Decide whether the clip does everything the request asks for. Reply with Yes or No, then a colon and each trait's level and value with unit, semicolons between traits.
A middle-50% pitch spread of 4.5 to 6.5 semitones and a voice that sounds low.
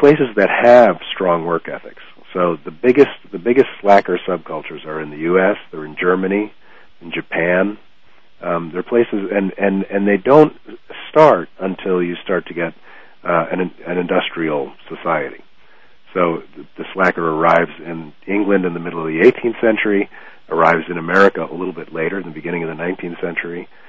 No: average, 3.0 semitones; very low, 90 Hz